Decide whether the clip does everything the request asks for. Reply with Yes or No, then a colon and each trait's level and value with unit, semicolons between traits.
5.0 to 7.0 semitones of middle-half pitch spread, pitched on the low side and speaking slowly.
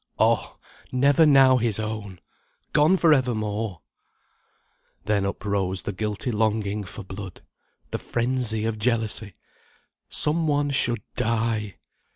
No: average, 3.8 semitones; low, 110 Hz; slow, 120 wpm